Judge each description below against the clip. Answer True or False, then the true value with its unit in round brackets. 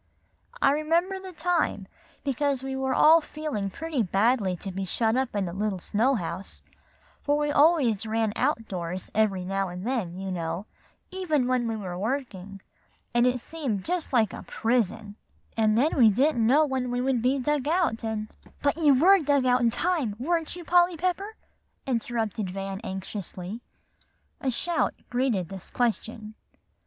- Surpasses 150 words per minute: True (165 wpm)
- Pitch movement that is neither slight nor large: False (6.3 semitones)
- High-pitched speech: True (240 Hz)